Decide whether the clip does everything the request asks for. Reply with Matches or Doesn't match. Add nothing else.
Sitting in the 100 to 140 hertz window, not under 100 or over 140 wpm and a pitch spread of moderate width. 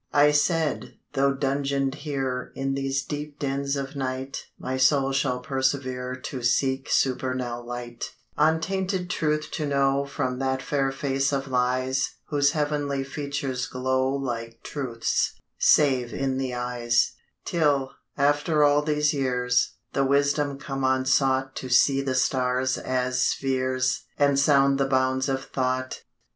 Doesn't match